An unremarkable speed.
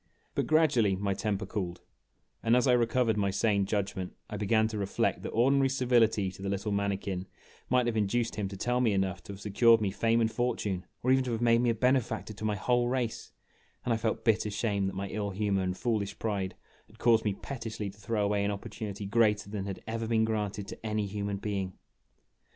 No: fast, 220 wpm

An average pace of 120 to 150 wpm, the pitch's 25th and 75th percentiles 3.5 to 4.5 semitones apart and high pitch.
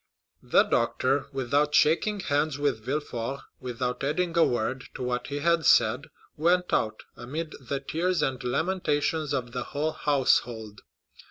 No: average, 145 wpm; average, 4.1 semitones; medium, 140 Hz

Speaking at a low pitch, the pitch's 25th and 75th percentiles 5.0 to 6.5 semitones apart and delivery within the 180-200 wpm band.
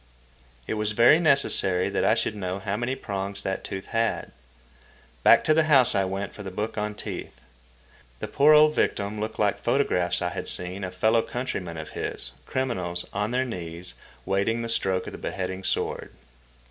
No: low, 105 Hz; average, 4.2 semitones; average, 185 wpm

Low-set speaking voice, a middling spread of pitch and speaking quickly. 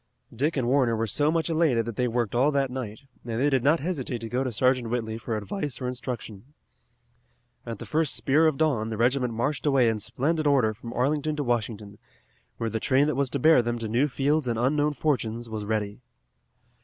Yes: low, 125 Hz; average, 4.1 semitones; fast, 215 wpm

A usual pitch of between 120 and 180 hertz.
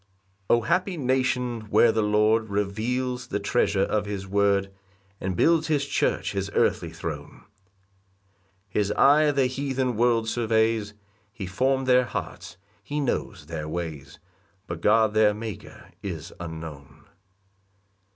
No: low, 110 Hz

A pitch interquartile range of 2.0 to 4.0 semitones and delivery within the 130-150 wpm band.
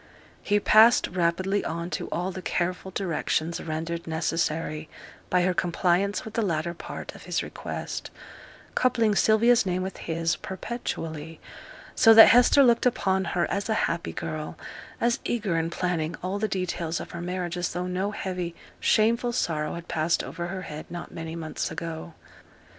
No: average, 3.4 semitones; average, 165 wpm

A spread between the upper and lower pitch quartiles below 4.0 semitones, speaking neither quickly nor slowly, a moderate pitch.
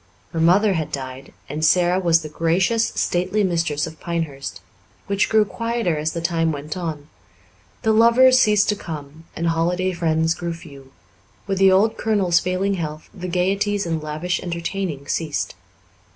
Yes: average, 3.6 semitones; average, 160 wpm; medium, 170 Hz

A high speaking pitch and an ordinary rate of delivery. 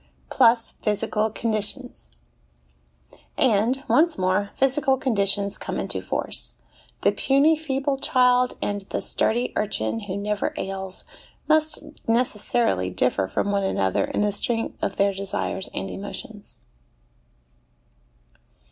No: high, 215 Hz; slow, 115 wpm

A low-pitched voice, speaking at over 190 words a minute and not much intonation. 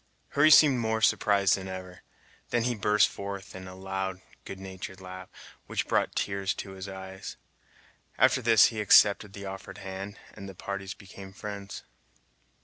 No: low, 100 Hz; average, 160 wpm; narrow, 1.6 semitones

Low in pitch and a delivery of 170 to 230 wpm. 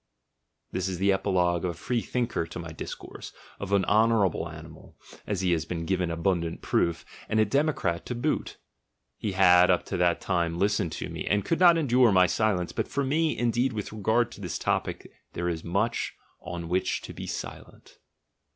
Yes: very low, 95 Hz; average, 185 wpm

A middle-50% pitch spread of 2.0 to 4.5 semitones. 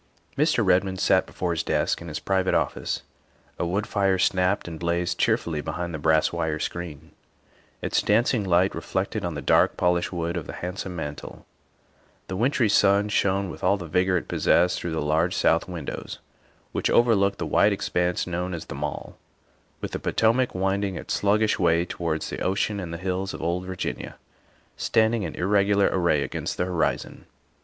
Yes: narrow, 2.6 semitones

